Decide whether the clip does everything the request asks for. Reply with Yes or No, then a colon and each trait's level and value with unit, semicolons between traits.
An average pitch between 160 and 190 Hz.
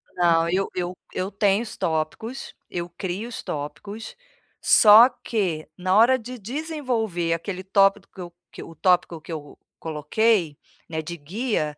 Yes: medium, 185 Hz